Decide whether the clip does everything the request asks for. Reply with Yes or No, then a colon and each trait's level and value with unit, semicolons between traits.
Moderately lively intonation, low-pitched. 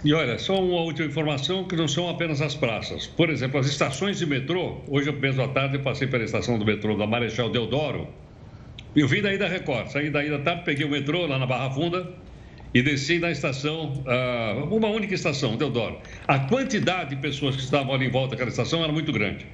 No: average, 4.7 semitones; medium, 145 Hz